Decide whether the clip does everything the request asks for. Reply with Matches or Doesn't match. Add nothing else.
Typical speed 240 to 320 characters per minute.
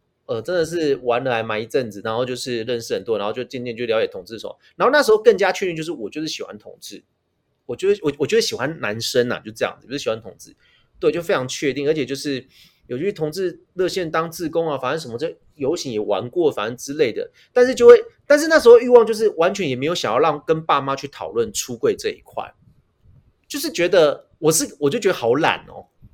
Doesn't match